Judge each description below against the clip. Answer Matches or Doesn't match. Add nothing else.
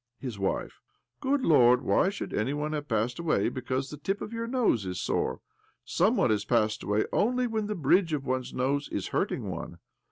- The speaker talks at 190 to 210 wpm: Matches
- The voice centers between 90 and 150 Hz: Matches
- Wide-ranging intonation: Matches